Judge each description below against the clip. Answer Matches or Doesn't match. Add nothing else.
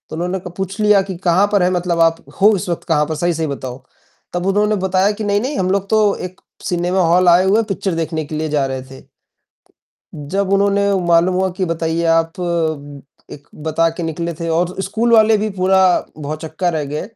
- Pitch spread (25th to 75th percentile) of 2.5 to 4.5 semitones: Matches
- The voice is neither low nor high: Matches